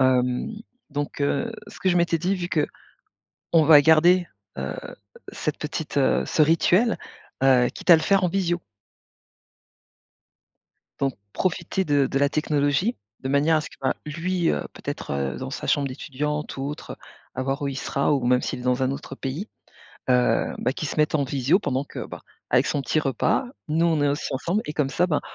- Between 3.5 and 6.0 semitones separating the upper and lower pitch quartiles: Yes, average, 3.8 semitones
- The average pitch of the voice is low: No, medium, 150 Hz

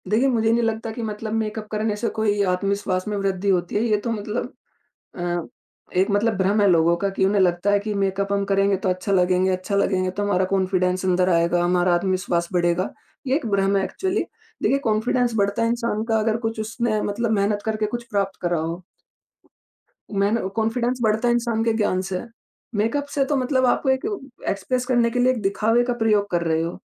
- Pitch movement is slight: No, average, 3.4 semitones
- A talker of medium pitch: No, high, 205 Hz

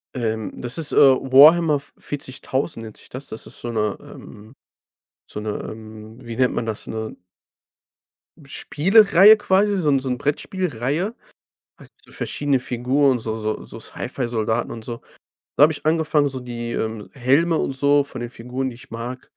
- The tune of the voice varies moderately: Yes, average, 4.2 semitones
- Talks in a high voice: No, low, 130 Hz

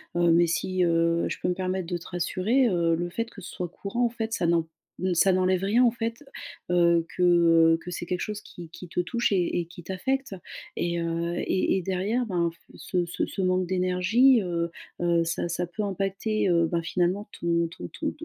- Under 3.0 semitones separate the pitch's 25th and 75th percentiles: Yes, narrow, 2.5 semitones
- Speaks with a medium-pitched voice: Yes, medium, 180 Hz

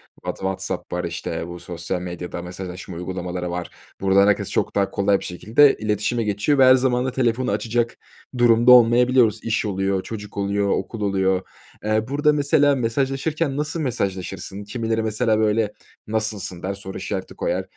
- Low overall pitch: Yes, low, 105 Hz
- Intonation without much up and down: No, average, 4.2 semitones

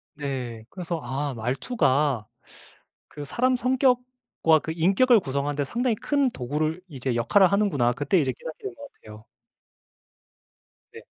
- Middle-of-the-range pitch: Yes, medium, 155 Hz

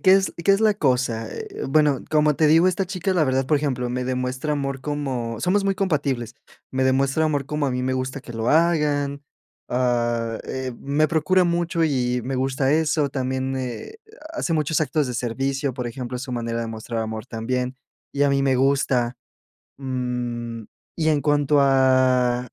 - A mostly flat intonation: No, average, 3.3 semitones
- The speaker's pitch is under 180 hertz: Yes, low, 135 Hz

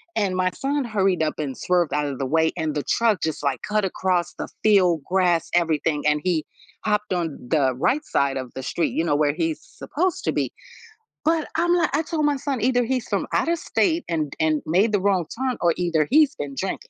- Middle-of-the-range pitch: Yes, medium, 180 Hz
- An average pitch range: No, wide, 7.4 semitones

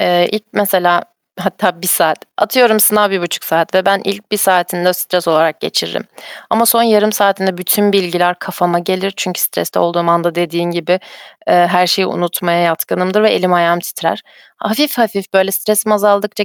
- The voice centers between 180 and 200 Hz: Yes, medium, 185 Hz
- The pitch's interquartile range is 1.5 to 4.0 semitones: Yes, average, 2.9 semitones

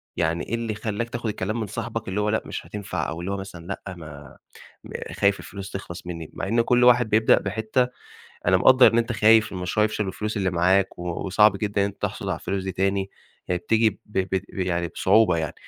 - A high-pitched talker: No, low, 100 Hz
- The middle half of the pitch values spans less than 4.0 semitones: Yes, average, 3.0 semitones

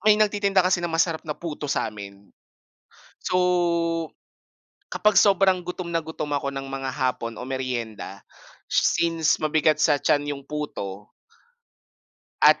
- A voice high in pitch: No, medium, 155 Hz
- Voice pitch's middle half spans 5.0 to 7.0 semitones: No, average, 4.6 semitones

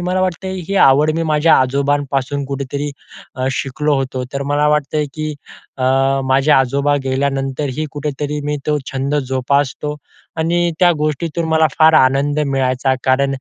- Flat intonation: Yes, narrow, 2.1 semitones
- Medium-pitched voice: Yes, medium, 145 Hz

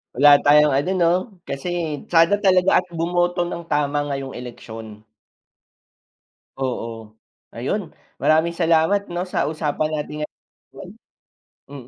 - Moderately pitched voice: Yes, medium, 150 Hz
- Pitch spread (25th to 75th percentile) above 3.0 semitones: Yes, average, 4.0 semitones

